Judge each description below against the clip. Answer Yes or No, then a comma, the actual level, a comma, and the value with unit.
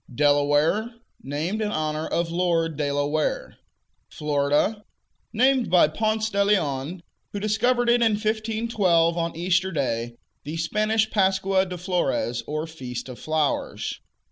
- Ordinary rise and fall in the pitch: No, wide, 6.0 semitones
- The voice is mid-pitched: Yes, medium, 170 Hz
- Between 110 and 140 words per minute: Yes, slow, 135 wpm